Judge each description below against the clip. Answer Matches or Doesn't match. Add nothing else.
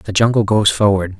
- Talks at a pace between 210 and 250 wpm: Doesn't match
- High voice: Doesn't match